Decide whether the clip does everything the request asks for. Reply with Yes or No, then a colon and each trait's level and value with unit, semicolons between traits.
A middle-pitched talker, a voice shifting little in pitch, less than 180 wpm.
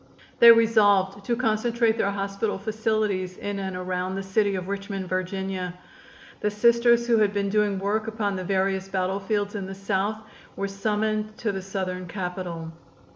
No: high, 200 Hz; narrow, 2.2 semitones; average, 160 wpm